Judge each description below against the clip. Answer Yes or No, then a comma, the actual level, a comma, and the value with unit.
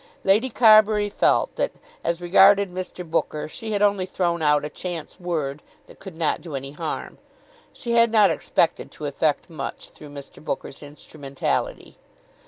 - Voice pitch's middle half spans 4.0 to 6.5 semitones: Yes, average, 5.2 semitones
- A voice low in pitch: No, medium, 175 Hz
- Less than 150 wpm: No, average, 160 wpm